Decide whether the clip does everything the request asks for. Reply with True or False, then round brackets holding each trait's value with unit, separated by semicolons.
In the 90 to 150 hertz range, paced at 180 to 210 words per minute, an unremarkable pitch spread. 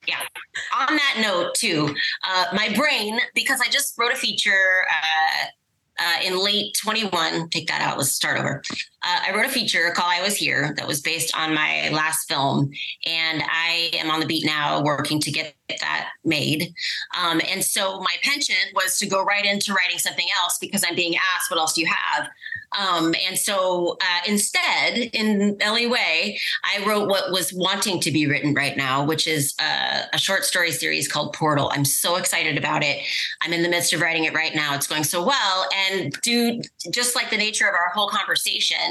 False (180 Hz; 200 wpm; 4.5 semitones)